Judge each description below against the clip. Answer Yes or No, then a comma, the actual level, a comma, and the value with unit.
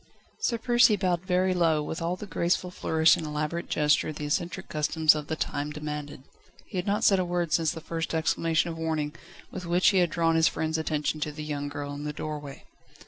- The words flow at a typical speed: No, fast, 215 wpm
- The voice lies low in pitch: No, medium, 160 Hz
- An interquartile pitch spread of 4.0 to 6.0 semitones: No, average, 2.8 semitones